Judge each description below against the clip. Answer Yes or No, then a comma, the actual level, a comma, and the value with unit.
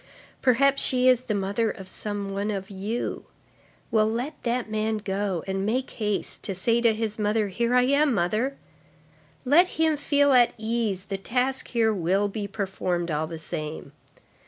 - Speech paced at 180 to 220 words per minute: No, average, 170 wpm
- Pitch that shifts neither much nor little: Yes, average, 4.2 semitones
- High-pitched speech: Yes, high, 215 Hz